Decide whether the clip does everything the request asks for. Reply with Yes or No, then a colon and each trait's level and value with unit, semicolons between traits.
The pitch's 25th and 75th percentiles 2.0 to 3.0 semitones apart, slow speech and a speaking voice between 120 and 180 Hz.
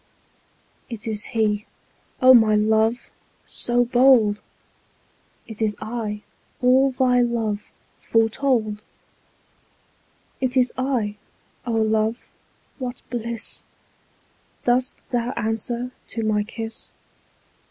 No: narrow, 2.4 semitones; slow, 90 wpm; high, 230 Hz